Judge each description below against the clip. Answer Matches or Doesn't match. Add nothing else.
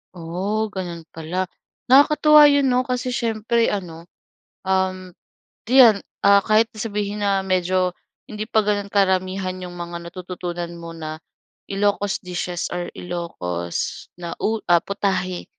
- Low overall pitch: Doesn't match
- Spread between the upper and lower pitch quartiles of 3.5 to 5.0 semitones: Doesn't match